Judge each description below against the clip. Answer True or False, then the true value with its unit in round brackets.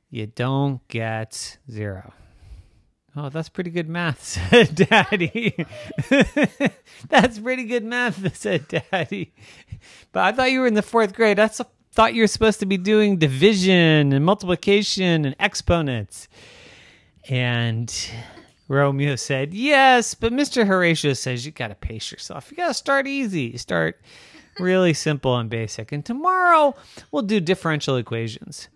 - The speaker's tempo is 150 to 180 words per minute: False (140 wpm)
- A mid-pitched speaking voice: True (170 Hz)